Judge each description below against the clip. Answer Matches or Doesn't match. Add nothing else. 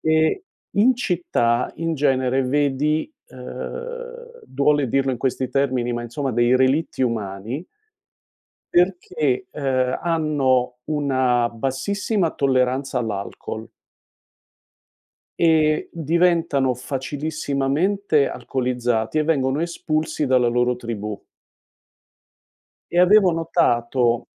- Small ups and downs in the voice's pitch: Doesn't match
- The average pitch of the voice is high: Doesn't match